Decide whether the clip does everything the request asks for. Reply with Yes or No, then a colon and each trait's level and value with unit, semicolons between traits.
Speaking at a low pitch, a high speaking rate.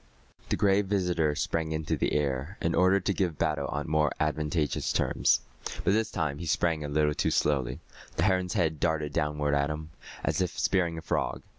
No: very low, 80 Hz; average, 190 wpm